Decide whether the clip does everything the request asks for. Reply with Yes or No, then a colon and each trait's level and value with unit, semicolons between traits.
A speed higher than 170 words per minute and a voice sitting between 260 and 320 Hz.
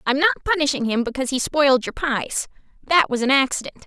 Yes: average, 200 wpm; very high, 275 Hz